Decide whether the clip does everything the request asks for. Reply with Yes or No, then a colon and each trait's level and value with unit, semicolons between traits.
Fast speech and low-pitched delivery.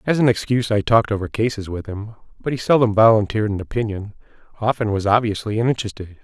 No: average, 185 wpm; low, 110 Hz